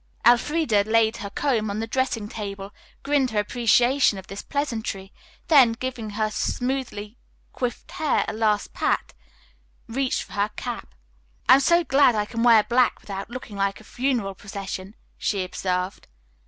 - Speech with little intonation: No, average, 3.9 semitones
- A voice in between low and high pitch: No, high, 225 Hz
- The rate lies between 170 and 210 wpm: No, average, 155 wpm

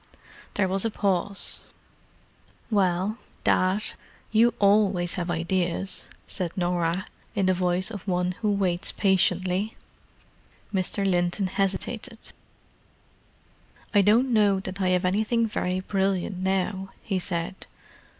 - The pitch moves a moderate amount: No, narrow, 2.0 semitones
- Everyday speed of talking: No, slow, 110 wpm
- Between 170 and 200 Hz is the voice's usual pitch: Yes, high, 190 Hz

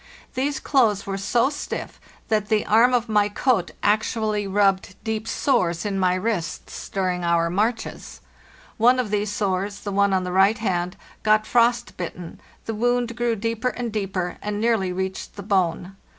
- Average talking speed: Yes, average, 160 wpm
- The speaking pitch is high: Yes, high, 210 Hz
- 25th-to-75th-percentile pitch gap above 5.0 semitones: No, average, 3.3 semitones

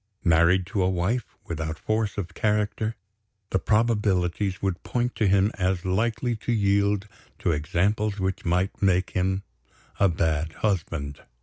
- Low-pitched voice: Yes, very low, 95 Hz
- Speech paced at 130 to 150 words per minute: Yes, average, 140 wpm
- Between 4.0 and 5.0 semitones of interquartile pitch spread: No, average, 3.2 semitones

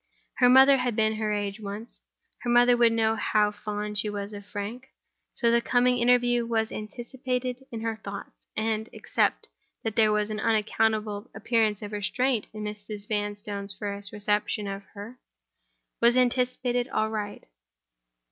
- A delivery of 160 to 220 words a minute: No, average, 145 wpm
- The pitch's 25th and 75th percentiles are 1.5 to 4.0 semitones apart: Yes, narrow, 2.6 semitones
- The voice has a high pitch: Yes, high, 220 Hz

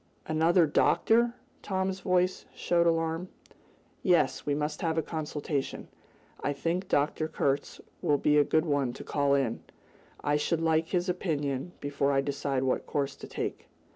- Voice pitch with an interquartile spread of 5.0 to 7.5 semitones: No, average, 3.3 semitones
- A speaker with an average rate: Yes, average, 160 wpm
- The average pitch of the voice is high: No, medium, 155 Hz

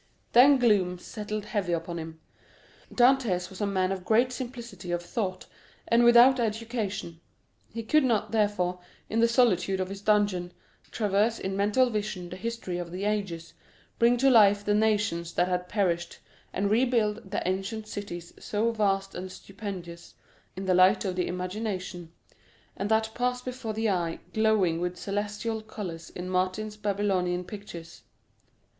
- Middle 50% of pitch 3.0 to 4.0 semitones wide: Yes, average, 3.4 semitones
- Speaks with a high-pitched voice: Yes, high, 205 Hz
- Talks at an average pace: Yes, average, 155 wpm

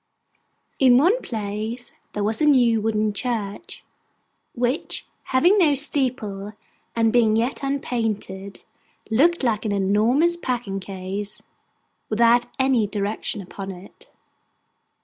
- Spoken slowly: Yes, slow, 110 wpm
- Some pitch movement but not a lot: Yes, average, 4.0 semitones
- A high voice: Yes, high, 225 Hz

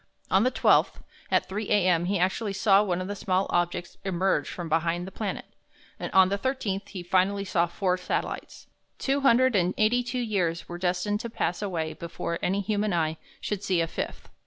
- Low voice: No, high, 190 Hz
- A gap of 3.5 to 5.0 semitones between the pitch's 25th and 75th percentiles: No, average, 3.0 semitones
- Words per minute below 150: No, average, 195 wpm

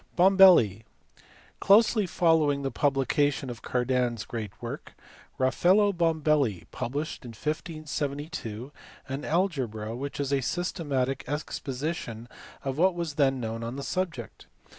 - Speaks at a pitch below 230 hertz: Yes, medium, 140 Hz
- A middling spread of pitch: Yes, average, 4.8 semitones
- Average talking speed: No, slow, 120 wpm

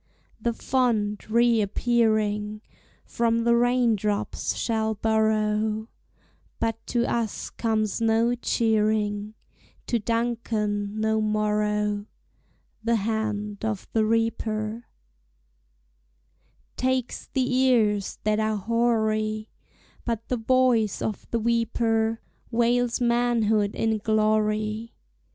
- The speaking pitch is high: Yes, high, 220 Hz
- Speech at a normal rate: No, slow, 95 wpm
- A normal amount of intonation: No, narrow, 1.6 semitones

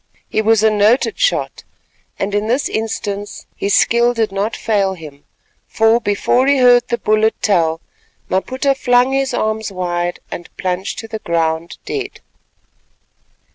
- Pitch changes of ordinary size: Yes, average, 4.0 semitones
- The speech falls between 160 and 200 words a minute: No, average, 145 wpm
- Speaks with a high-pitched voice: Yes, high, 215 Hz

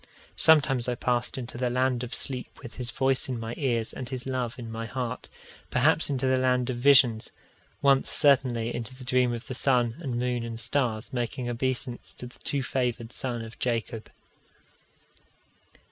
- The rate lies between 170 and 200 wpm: Yes, average, 175 wpm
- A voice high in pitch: No, low, 125 Hz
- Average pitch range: No, narrow, 1.7 semitones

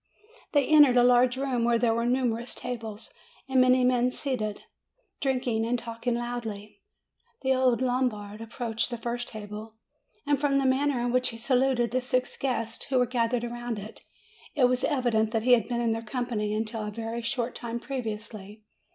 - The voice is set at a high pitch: Yes, high, 240 Hz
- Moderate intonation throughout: No, narrow, 2.0 semitones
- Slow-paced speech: No, average, 185 wpm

